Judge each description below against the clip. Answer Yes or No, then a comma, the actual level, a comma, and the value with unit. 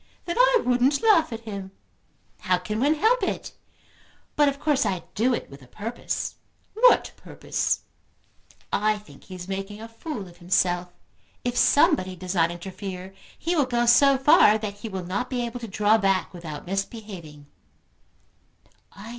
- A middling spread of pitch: No, wide, 5.9 semitones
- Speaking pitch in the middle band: No, high, 215 Hz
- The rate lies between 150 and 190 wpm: Yes, average, 165 wpm